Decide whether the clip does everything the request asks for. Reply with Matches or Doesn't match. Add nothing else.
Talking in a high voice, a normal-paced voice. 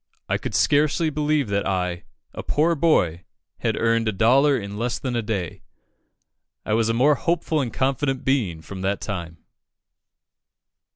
Doesn't match